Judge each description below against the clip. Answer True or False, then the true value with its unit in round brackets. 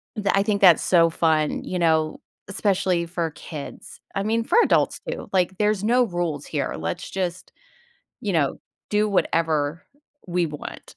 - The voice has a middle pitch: True (175 Hz)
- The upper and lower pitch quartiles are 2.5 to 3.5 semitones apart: False (3.9 semitones)